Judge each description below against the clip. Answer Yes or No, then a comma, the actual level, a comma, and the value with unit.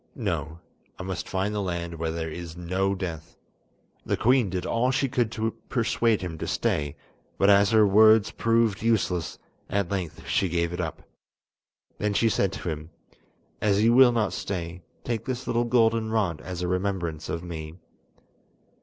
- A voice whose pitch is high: No, very low, 95 Hz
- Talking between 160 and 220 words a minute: Yes, average, 170 wpm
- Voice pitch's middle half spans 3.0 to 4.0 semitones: No, average, 4.6 semitones